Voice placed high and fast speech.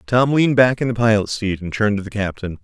No: low, 110 Hz; fast, 275 wpm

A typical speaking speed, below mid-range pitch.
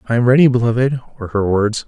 Yes: average, 190 wpm; low, 120 Hz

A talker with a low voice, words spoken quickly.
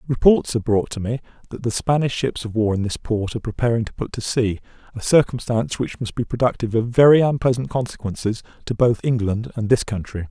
Yes: low, 115 Hz; fast, 210 wpm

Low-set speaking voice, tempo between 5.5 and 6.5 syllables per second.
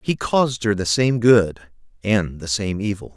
No: low, 105 Hz; 4.6 syllables/s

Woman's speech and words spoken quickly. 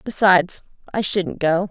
No: female; average, 140 wpm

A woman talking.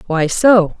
Yes: female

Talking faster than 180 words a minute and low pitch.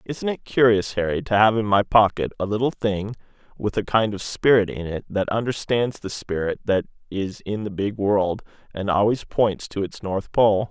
Yes: average, 200 wpm; low, 105 Hz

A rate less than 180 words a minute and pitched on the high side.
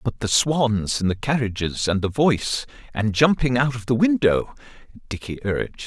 No: average, 165 wpm; low, 120 Hz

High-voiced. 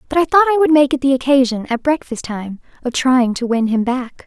Yes: very high, 265 Hz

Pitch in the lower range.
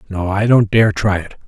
Yes: low, 100 Hz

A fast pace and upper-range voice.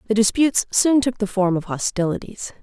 No: average, 185 wpm; high, 215 Hz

